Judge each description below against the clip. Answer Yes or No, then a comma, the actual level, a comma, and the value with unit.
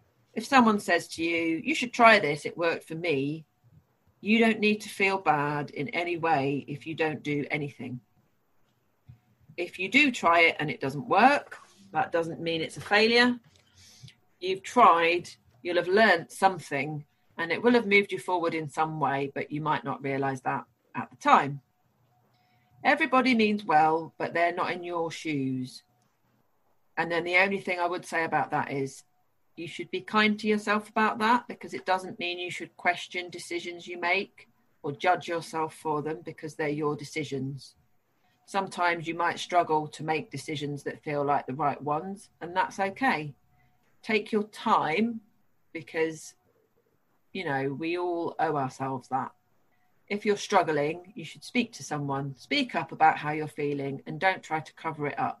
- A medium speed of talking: Yes, average, 175 wpm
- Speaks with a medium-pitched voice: Yes, medium, 165 Hz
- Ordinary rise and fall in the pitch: Yes, average, 4.8 semitones